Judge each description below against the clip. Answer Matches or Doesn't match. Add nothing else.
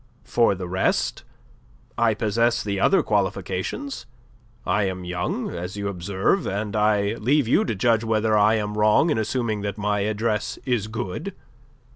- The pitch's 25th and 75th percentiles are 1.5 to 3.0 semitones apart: Matches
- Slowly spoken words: Doesn't match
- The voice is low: Matches